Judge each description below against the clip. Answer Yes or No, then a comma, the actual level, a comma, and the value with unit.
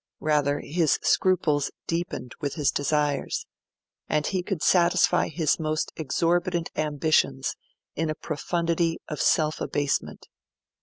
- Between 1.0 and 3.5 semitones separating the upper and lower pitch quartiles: Yes, narrow, 2.5 semitones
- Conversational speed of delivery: No, slow, 115 wpm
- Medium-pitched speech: Yes, medium, 155 Hz